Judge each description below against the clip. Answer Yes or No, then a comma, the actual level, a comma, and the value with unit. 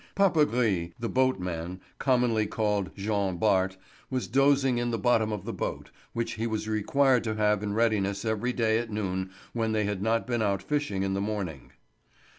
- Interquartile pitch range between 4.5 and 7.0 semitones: No, average, 3.3 semitones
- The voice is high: No, low, 110 Hz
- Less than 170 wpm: No, average, 180 wpm